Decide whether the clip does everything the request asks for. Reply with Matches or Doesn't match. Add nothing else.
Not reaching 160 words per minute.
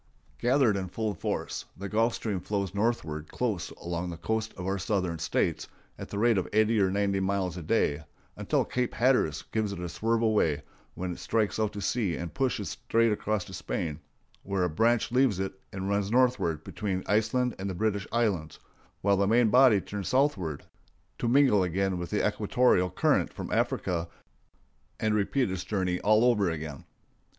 Doesn't match